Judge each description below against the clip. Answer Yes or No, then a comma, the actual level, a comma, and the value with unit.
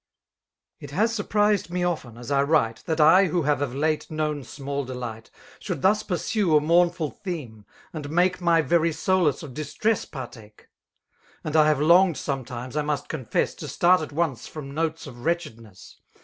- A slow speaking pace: No, average, 175 wpm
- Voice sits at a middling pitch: Yes, medium, 155 Hz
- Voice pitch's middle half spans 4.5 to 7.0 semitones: No, average, 4.1 semitones